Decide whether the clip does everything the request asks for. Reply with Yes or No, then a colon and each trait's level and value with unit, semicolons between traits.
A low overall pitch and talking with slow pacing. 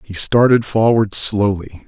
Yes: low, 105 Hz; slow, 130 wpm